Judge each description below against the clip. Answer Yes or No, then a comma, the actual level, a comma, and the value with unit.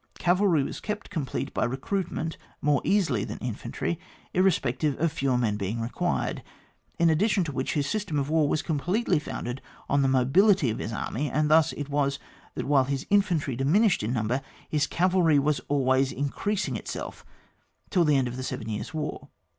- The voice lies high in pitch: No, medium, 145 Hz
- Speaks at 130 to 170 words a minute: No, average, 185 wpm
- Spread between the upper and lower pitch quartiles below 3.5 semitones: No, average, 4.6 semitones